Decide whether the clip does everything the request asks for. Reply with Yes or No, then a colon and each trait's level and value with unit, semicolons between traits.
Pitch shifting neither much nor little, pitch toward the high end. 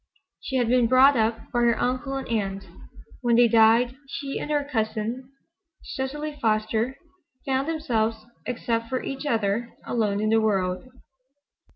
Yes: average, 3.2 semitones; high, 235 Hz